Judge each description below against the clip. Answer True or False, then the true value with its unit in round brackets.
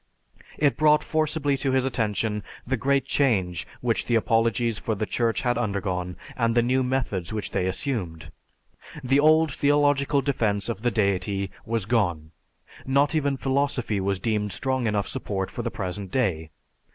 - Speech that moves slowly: False (160 wpm)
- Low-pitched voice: True (115 Hz)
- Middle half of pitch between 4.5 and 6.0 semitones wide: True (5.2 semitones)